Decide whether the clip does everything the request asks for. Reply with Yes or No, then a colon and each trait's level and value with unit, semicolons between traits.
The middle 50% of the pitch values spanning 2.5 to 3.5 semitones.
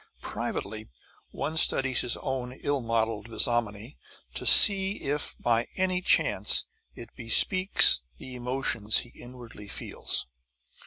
No: average, 4.1 semitones